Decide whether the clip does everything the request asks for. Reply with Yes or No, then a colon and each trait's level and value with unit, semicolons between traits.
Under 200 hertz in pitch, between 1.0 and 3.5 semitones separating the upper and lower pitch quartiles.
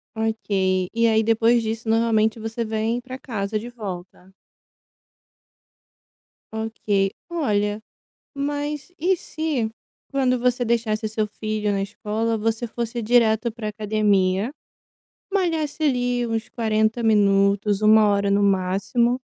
No: high, 220 Hz; narrow, 2.5 semitones